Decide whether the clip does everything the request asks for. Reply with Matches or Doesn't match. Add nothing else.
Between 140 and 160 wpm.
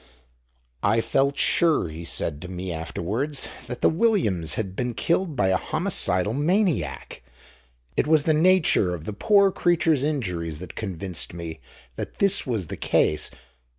Matches